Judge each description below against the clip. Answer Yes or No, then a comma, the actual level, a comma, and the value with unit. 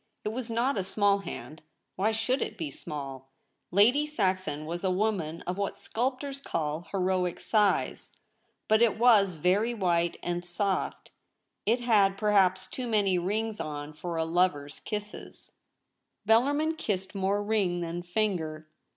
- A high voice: Yes, high, 195 Hz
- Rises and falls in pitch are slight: No, average, 4.1 semitones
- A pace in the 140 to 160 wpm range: Yes, average, 155 wpm